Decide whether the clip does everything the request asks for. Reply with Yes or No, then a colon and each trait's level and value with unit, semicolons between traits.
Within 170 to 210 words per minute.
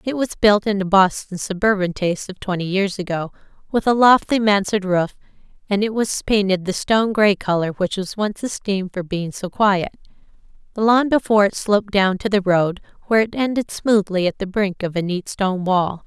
Yes: average, 200 wpm